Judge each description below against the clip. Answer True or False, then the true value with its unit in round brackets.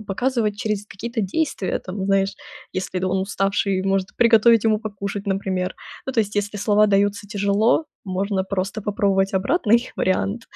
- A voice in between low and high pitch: False (200 Hz)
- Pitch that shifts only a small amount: True (2.0 semitones)